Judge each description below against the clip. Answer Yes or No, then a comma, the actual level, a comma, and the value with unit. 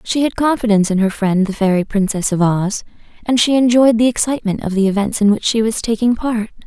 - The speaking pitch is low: No, high, 215 Hz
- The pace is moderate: No, fast, 225 wpm